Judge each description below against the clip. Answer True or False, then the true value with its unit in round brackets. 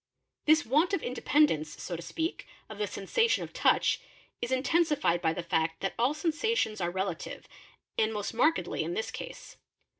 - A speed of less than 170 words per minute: False (175 wpm)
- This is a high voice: True (240 Hz)